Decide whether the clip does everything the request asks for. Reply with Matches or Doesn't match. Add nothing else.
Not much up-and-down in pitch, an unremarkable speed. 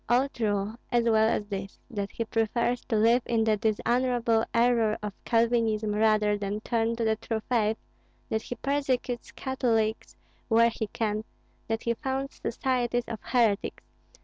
Matches